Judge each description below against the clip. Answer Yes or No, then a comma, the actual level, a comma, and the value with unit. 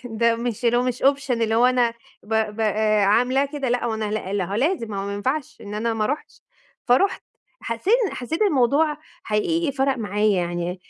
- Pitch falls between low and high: No, high, 235 Hz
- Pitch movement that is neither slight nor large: Yes, average, 4.0 semitones